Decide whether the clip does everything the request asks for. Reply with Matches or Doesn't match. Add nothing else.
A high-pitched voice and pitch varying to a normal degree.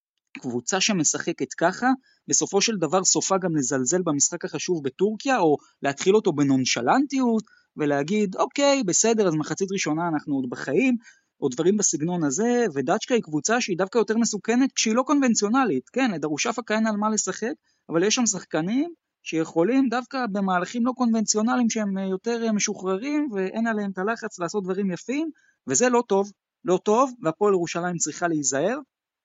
Doesn't match